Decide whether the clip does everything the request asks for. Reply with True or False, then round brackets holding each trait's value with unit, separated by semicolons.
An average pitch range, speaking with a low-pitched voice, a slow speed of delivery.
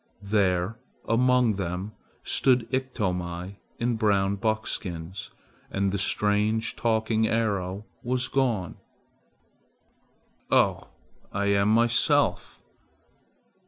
True (3.0 semitones; 105 Hz; 85 wpm)